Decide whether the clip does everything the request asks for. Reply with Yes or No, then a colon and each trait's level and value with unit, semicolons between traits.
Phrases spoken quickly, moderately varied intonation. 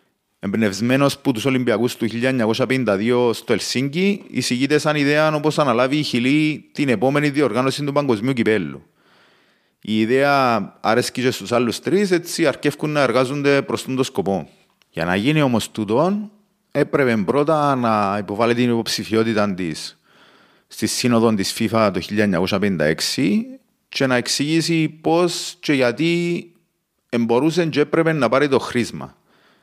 No: average, 135 wpm; average, 4.6 semitones